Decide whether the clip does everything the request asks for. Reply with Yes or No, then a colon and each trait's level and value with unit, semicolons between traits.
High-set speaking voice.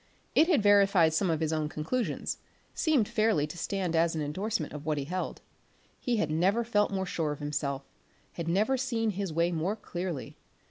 No: medium, 180 Hz